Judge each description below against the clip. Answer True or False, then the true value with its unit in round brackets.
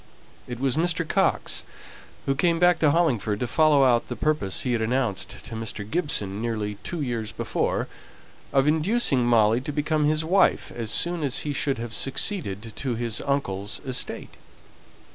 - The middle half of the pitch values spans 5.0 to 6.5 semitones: True (5.5 semitones)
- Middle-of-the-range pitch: False (130 Hz)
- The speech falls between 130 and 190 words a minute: True (165 wpm)